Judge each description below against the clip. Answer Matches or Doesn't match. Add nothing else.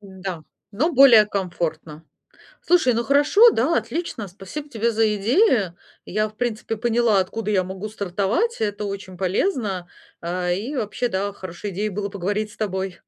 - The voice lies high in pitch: Matches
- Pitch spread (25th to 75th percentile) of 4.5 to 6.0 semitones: Doesn't match